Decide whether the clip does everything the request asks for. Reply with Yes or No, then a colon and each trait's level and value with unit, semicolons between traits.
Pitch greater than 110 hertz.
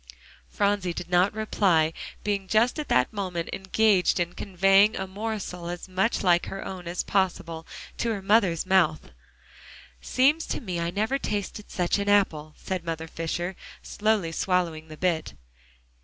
Yes: medium, 185 Hz